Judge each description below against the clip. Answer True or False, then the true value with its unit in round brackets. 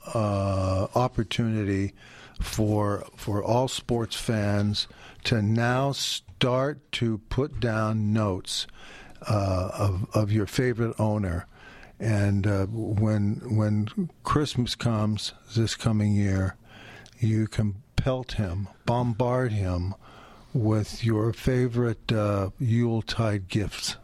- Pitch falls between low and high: False (110 Hz)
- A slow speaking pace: True (105 wpm)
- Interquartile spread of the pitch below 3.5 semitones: True (2.7 semitones)